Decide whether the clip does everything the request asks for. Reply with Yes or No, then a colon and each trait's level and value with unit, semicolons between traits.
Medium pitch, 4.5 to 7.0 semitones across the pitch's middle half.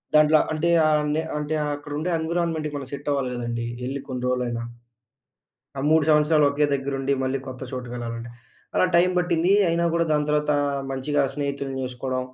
No: medium, 145 Hz; average, 3.0 semitones